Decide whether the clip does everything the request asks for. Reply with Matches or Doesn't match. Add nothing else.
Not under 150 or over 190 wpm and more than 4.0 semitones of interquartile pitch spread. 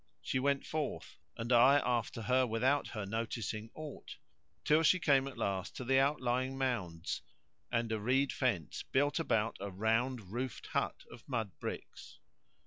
Doesn't match